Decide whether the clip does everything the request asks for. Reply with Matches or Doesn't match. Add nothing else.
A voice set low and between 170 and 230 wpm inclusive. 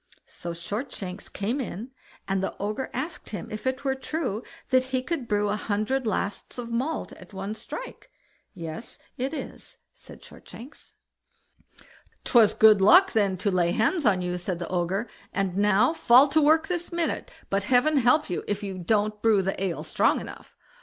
Doesn't match